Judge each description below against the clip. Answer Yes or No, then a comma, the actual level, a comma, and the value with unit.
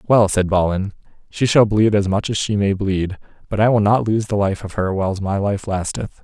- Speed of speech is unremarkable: No, fast, 240 wpm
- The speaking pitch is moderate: No, low, 100 Hz